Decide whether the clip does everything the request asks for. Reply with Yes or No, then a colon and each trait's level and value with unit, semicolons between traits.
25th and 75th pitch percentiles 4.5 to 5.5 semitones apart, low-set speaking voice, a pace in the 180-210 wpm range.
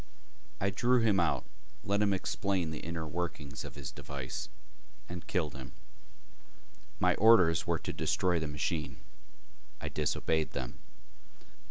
No: average, 4.9 semitones; very low, 85 Hz; slow, 135 wpm